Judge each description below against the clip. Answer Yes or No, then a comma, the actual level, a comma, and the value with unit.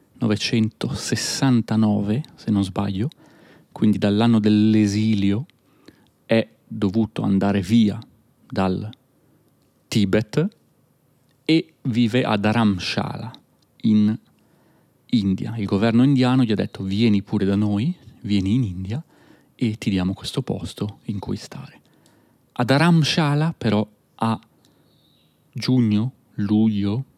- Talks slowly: Yes, slow, 100 wpm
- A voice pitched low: Yes, low, 110 Hz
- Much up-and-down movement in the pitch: No, average, 3.9 semitones